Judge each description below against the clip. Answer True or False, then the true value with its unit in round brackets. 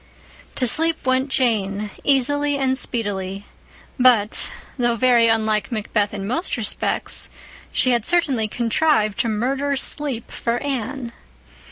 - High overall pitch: True (240 Hz)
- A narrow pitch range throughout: False (3.9 semitones)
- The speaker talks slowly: True (125 wpm)